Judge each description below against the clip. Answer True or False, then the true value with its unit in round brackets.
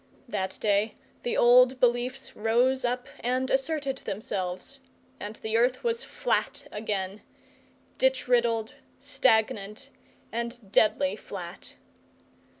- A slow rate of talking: True (105 wpm)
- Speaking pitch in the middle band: False (240 Hz)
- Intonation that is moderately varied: True (3.5 semitones)